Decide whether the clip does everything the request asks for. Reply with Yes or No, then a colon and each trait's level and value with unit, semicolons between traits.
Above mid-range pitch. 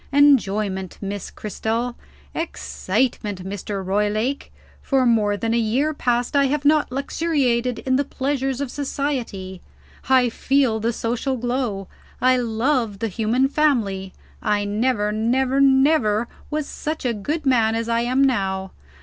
Yes: high, 240 Hz